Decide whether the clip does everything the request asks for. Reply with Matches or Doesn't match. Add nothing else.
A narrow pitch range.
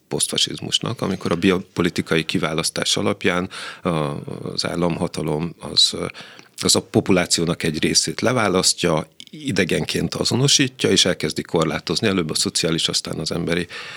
Matches